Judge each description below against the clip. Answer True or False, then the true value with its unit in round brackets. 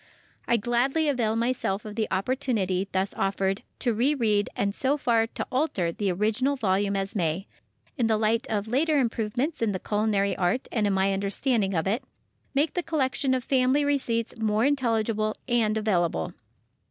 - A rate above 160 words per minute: True (170 wpm)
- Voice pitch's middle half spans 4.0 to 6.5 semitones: True (4.4 semitones)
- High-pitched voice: True (220 Hz)